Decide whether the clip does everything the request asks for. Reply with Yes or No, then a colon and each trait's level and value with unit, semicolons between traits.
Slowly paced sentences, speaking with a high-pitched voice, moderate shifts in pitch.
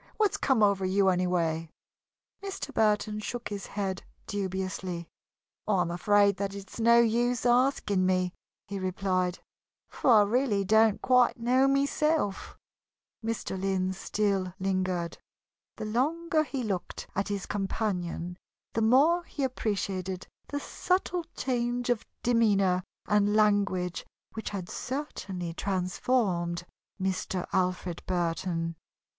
Yes: slow, 120 wpm; high, 200 Hz; average, 4.4 semitones